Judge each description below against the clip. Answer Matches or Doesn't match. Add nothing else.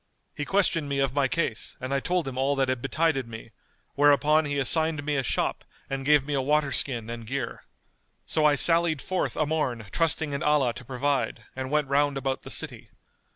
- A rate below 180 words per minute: Doesn't match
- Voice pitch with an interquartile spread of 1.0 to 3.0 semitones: Matches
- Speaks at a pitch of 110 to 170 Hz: Matches